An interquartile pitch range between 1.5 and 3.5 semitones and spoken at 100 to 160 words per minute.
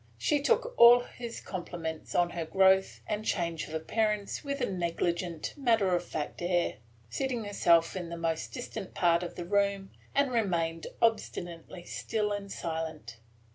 No: average, 4.5 semitones; average, 155 wpm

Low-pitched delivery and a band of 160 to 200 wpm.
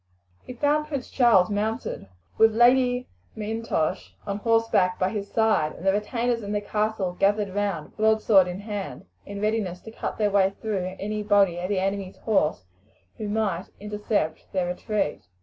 No: high, 205 Hz; average, 165 wpm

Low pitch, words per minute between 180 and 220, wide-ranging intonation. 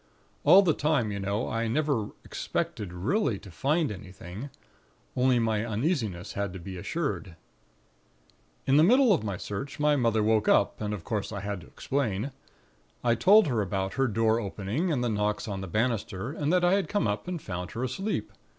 Yes: low, 110 Hz; average, 190 wpm; wide, 6.3 semitones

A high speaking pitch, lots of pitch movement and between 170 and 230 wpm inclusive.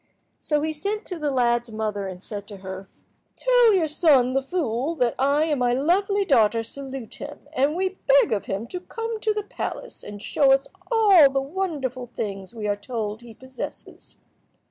Yes: very high, 270 Hz; wide, 6.8 semitones; average, 190 wpm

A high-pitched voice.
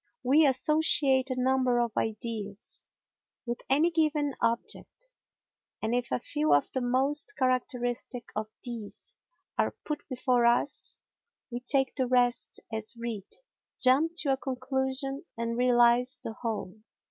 Yes: very high, 255 Hz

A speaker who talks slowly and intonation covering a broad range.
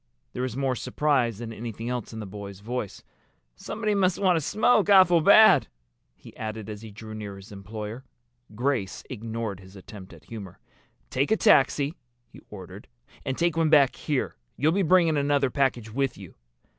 No: average, 175 wpm; wide, 6.2 semitones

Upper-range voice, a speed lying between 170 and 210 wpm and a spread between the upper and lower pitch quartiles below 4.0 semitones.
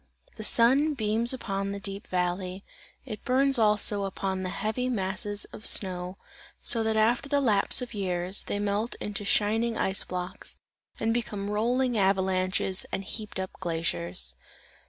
No: high, 205 Hz; average, 150 wpm; average, 3.2 semitones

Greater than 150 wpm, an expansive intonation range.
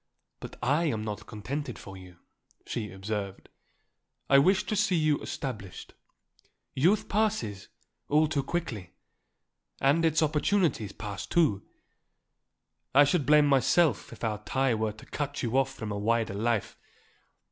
No: average, 140 wpm; wide, 6.4 semitones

